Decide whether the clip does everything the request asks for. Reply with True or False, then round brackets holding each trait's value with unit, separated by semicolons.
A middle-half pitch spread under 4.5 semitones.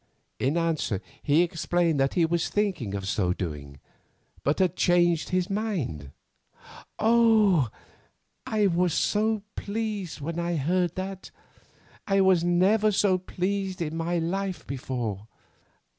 False (4.9 semitones)